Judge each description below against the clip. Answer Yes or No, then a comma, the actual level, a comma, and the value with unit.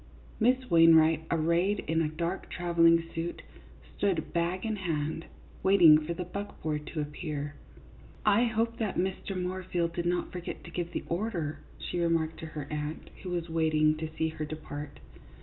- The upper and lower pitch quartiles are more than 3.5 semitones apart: No, narrow, 2.6 semitones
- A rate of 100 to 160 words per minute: No, average, 170 wpm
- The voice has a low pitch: No, medium, 170 Hz